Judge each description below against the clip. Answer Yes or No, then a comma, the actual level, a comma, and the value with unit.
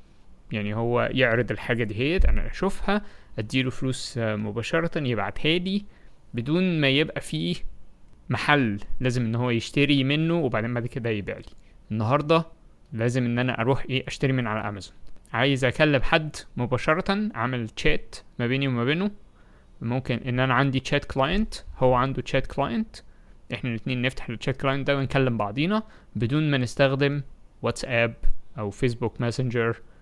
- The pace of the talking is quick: Yes, fast, 145 wpm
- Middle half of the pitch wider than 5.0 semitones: No, average, 3.7 semitones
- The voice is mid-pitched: No, low, 130 Hz